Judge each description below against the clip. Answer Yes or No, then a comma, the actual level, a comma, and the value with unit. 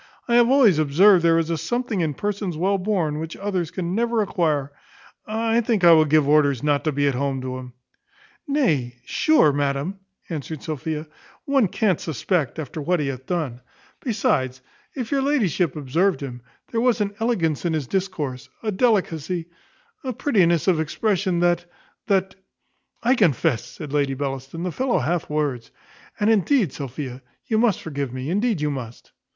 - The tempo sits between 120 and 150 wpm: No, average, 170 wpm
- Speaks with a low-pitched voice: No, medium, 165 Hz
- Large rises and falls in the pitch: Yes, wide, 6.4 semitones